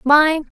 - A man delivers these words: No, female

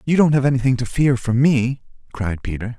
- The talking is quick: Yes, fast, 215 wpm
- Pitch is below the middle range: Yes, low, 125 Hz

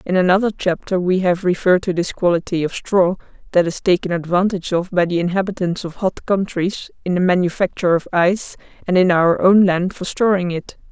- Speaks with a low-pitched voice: No, medium, 180 Hz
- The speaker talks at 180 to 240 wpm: Yes, average, 190 wpm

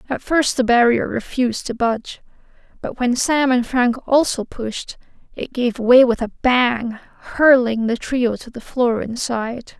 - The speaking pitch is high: Yes, high, 245 Hz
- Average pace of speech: Yes, average, 165 wpm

